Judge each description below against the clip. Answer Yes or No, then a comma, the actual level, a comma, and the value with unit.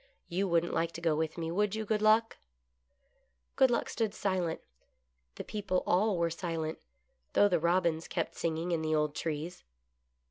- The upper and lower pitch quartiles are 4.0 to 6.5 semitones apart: No, average, 3.6 semitones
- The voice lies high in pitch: No, medium, 170 Hz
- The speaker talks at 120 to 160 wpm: No, average, 180 wpm